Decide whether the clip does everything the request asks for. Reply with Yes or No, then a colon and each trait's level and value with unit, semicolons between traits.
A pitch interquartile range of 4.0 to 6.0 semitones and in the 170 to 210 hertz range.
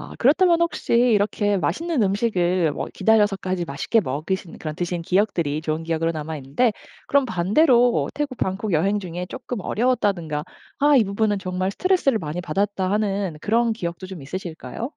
Yes: average, 5.3 semitones; high, 195 Hz